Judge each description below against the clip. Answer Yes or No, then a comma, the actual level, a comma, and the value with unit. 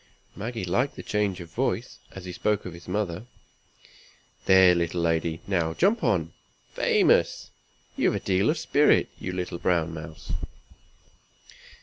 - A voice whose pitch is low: Yes, very low, 90 Hz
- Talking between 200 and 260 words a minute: No, average, 140 wpm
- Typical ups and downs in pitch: Yes, average, 3.7 semitones